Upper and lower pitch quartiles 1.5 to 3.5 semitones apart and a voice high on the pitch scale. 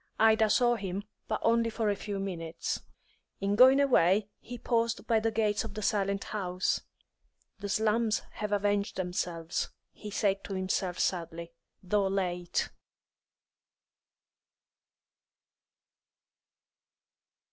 Yes: average, 2.8 semitones; high, 205 Hz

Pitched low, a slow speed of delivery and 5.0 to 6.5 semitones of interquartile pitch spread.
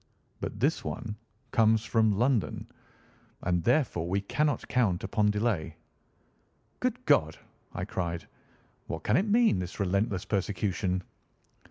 No: low, 105 Hz; slow, 125 wpm; average, 4.2 semitones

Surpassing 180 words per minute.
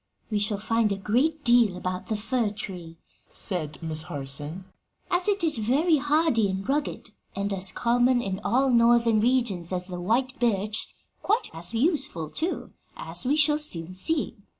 No: average, 165 wpm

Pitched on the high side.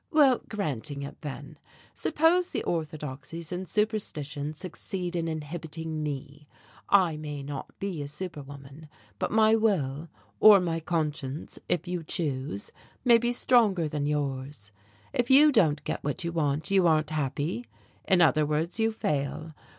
No: medium, 160 Hz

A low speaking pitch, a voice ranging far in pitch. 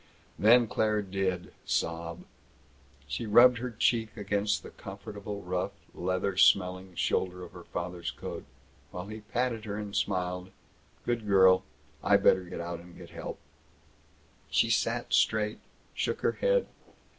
No: low, 100 Hz; average, 3.1 semitones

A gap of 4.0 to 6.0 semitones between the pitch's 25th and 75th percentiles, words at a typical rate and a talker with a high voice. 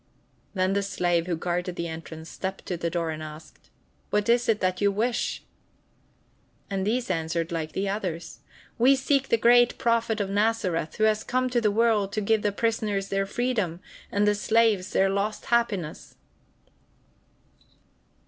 Yes: average, 4.4 semitones; average, 165 wpm; high, 200 Hz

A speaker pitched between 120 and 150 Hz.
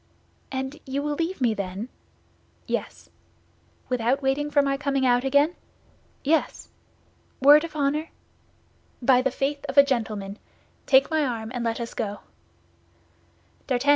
No: very high, 270 Hz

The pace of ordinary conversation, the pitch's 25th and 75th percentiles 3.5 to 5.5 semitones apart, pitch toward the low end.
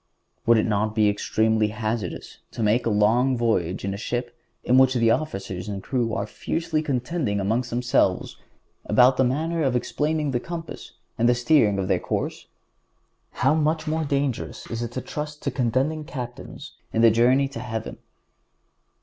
Yes: average, 165 wpm; average, 4.2 semitones; low, 120 Hz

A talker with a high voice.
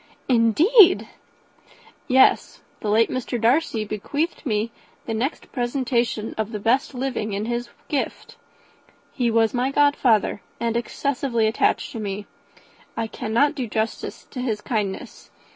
Yes: high, 235 Hz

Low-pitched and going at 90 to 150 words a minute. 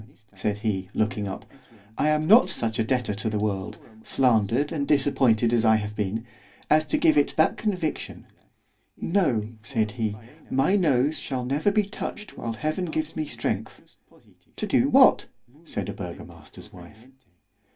Yes: low, 115 Hz; average, 140 wpm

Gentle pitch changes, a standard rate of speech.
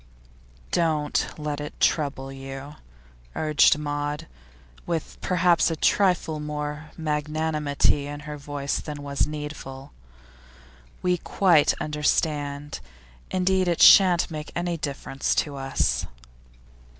No: narrow, 1.9 semitones; slow, 110 wpm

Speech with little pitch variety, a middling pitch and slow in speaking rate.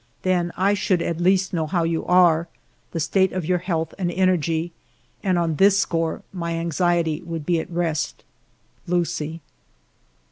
No: narrow, 1.9 semitones; medium, 170 Hz; average, 155 wpm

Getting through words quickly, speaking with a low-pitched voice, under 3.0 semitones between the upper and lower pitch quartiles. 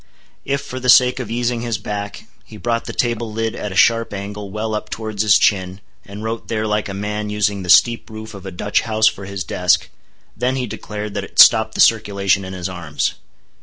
Yes: fast, 215 wpm; low, 105 Hz; narrow, 2.4 semitones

